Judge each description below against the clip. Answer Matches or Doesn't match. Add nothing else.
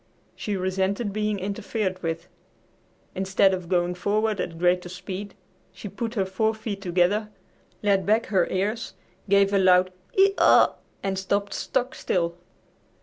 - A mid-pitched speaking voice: Doesn't match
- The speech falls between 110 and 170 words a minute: Matches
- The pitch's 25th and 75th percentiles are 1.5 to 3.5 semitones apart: Matches